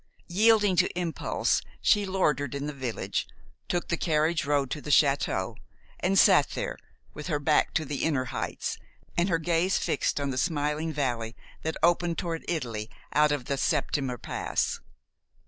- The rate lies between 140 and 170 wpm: Yes, average, 165 wpm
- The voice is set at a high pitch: No, medium, 150 Hz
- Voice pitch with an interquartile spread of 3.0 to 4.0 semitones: Yes, average, 3.6 semitones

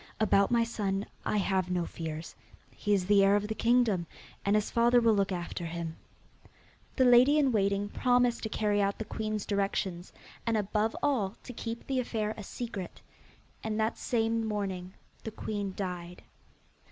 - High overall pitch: Yes, high, 210 Hz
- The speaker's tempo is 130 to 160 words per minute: No, average, 170 wpm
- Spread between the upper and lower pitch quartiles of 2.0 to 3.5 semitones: Yes, average, 2.8 semitones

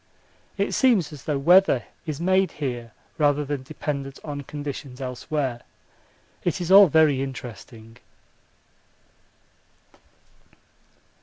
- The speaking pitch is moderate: Yes, medium, 145 Hz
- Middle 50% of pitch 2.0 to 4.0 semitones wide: Yes, average, 3.5 semitones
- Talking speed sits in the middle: No, slow, 100 wpm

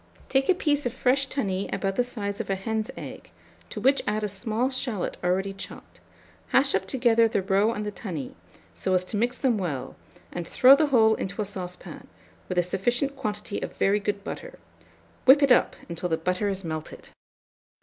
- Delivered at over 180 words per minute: Yes, average, 195 wpm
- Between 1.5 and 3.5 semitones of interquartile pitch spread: No, average, 4.7 semitones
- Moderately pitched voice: No, high, 210 Hz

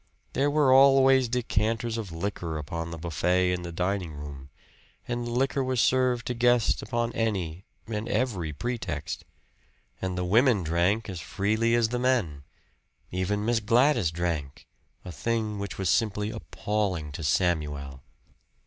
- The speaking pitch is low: Yes, low, 105 Hz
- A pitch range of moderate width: No, wide, 5.8 semitones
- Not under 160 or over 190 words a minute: No, average, 145 wpm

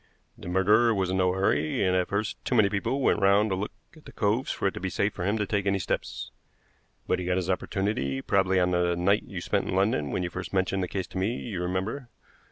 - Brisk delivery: Yes, fast, 255 wpm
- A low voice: Yes, very low, 95 Hz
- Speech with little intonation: Yes, narrow, 2.1 semitones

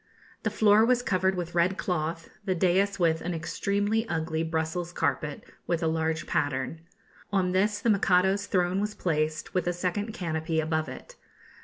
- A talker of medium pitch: Yes, medium, 175 Hz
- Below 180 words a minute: Yes, average, 165 wpm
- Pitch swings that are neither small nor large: Yes, average, 3.6 semitones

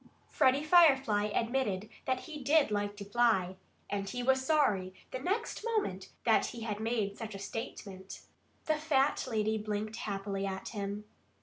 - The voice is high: Yes, high, 220 Hz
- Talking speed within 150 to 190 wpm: Yes, average, 165 wpm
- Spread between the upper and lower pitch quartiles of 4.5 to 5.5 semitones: Yes, average, 4.8 semitones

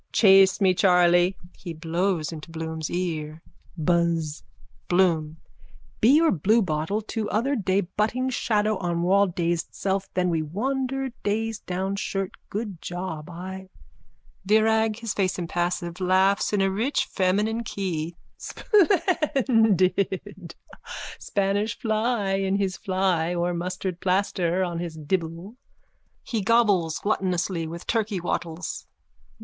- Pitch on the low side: No, high, 190 Hz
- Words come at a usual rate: No, slow, 120 wpm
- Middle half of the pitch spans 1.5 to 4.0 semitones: Yes, average, 3.6 semitones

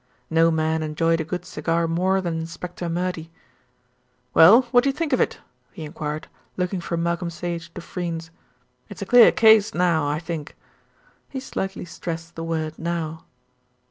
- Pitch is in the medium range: Yes, medium, 170 Hz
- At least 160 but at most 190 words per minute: Yes, average, 165 wpm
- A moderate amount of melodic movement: No, narrow, 1.8 semitones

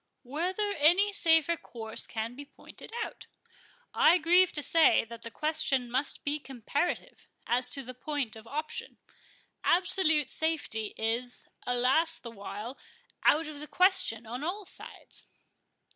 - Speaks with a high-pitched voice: Yes, very high, 290 Hz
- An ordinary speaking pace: No, slow, 130 wpm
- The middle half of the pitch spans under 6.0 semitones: Yes, wide, 5.5 semitones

